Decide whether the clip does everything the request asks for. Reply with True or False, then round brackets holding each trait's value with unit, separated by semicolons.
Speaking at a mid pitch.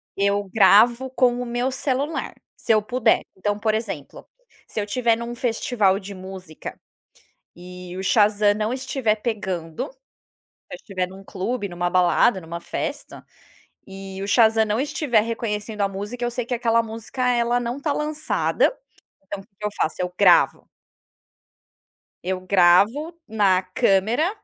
False (215 Hz)